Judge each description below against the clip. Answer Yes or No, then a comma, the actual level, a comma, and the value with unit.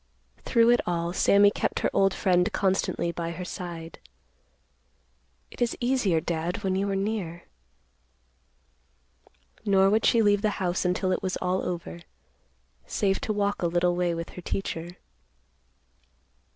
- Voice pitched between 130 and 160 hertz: No, medium, 185 Hz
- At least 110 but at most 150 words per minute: Yes, average, 145 wpm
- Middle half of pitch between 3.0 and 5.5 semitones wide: No, narrow, 2.6 semitones